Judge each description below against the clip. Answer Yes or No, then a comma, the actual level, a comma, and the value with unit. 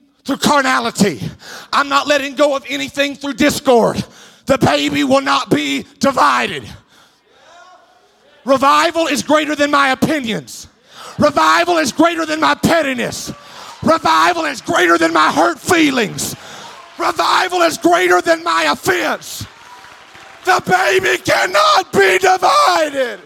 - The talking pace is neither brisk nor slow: No, slow, 120 wpm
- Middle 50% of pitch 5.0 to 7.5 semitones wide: No, average, 3.7 semitones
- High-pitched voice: Yes, very high, 290 Hz